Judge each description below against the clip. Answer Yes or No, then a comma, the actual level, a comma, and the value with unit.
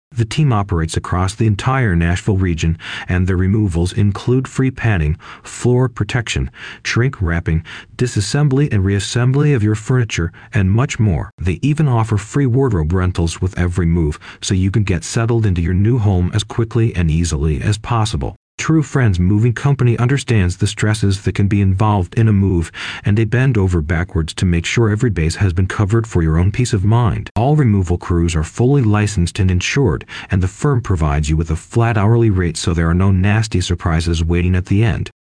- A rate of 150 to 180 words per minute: No, average, 190 wpm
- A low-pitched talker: Yes, low, 105 Hz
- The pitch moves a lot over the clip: No, average, 4.8 semitones